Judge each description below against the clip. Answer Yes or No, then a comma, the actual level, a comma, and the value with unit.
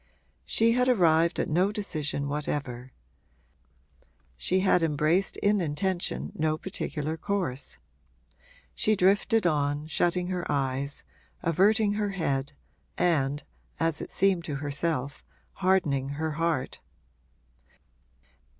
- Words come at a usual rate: No, slow, 105 wpm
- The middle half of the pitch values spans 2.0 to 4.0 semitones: No, average, 4.7 semitones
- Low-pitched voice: No, medium, 160 Hz